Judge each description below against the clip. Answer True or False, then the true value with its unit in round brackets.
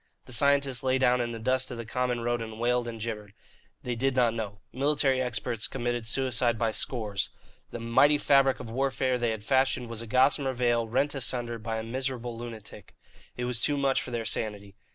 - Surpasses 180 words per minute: True (200 wpm)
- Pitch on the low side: True (120 Hz)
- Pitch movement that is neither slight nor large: False (2.3 semitones)